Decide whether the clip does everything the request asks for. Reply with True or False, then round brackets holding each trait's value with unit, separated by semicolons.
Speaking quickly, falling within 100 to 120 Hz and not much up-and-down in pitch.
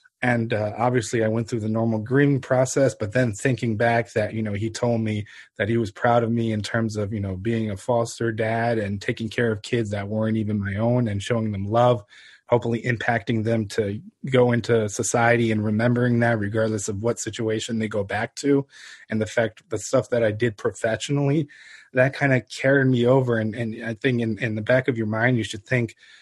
True (220 wpm; 115 Hz; 2.0 semitones)